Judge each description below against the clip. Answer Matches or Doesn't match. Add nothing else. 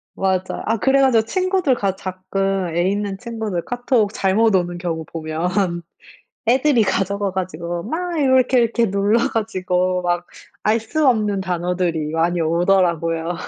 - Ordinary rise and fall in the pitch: Matches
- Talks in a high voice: Matches